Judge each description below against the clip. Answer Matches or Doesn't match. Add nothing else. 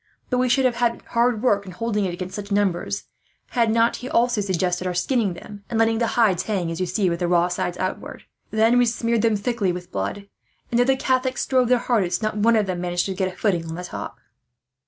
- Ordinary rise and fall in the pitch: Matches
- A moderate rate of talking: Doesn't match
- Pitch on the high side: Matches